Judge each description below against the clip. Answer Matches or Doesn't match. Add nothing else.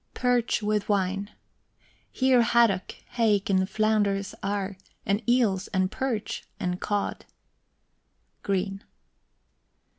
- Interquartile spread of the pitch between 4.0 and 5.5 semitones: Doesn't match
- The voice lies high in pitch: Matches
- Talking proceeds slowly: Matches